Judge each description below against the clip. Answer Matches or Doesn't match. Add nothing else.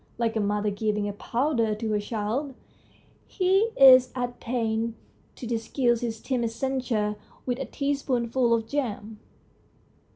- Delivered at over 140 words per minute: Doesn't match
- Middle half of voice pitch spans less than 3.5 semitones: Matches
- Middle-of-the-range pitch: Doesn't match